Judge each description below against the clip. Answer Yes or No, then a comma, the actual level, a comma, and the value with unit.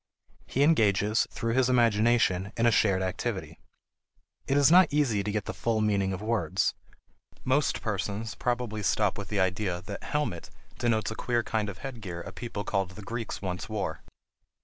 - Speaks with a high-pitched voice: No, low, 110 Hz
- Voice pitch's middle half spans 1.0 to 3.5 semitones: Yes, average, 3.2 semitones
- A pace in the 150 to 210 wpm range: Yes, average, 170 wpm